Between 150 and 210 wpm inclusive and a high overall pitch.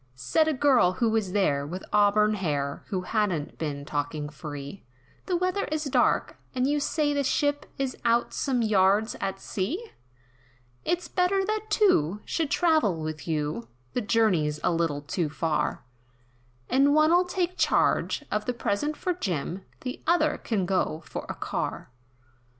Yes: average, 155 wpm; high, 210 Hz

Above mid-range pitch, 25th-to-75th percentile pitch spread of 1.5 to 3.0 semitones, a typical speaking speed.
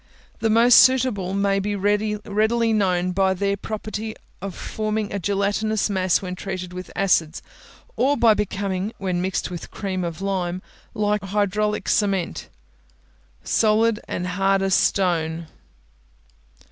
No: high, 200 Hz; narrow, 2.5 semitones; slow, 130 wpm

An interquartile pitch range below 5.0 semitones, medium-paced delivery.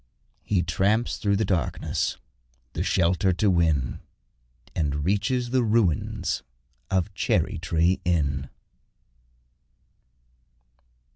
No: average, 4.2 semitones; slow, 90 wpm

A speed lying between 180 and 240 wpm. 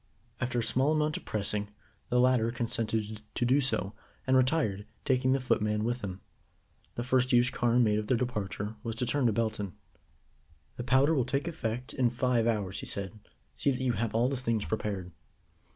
Yes: average, 190 wpm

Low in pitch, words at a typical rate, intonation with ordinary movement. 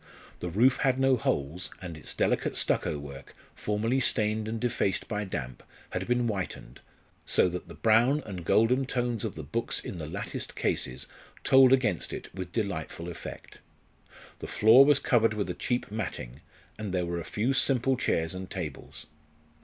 No: low, 105 Hz; average, 170 wpm; wide, 5.9 semitones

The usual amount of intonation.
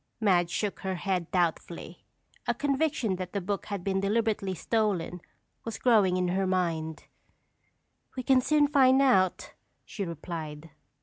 Yes: average, 4.3 semitones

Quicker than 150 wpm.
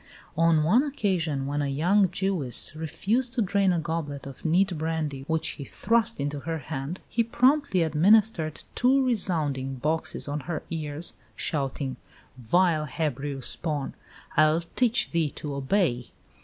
No: average, 140 wpm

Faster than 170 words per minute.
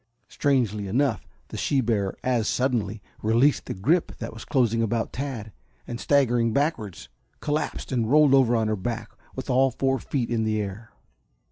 No: average, 165 wpm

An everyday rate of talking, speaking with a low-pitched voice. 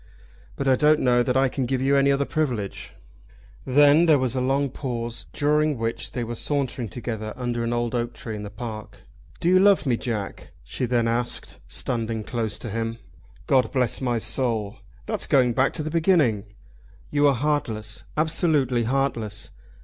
Yes: average, 180 wpm; low, 125 Hz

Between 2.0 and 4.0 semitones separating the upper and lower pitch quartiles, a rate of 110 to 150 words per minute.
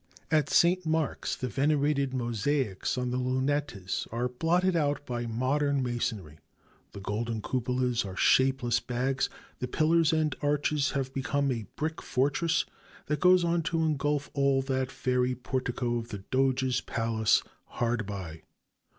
Yes: average, 3.5 semitones; average, 140 wpm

